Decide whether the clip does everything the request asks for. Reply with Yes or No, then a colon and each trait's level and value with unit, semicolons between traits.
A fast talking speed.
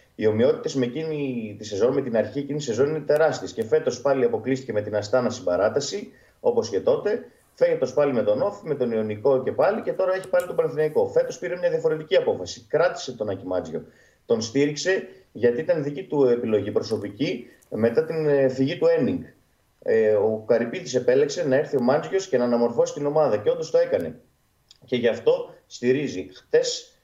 Yes: fast, 185 wpm